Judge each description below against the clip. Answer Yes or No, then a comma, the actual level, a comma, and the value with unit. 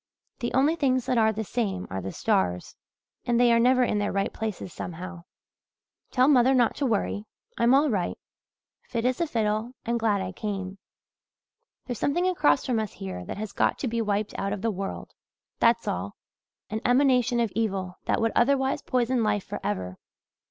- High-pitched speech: Yes, high, 225 Hz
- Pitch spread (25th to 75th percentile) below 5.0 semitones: Yes, average, 4.1 semitones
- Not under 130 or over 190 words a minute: Yes, average, 185 wpm